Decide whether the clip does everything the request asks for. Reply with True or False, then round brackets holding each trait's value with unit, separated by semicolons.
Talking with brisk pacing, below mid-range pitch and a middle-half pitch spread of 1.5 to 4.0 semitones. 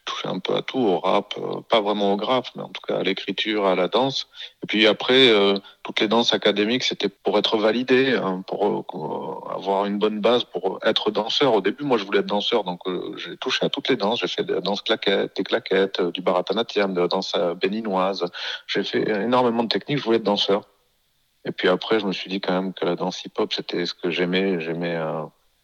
True (235 wpm; 100 Hz; 3.2 semitones)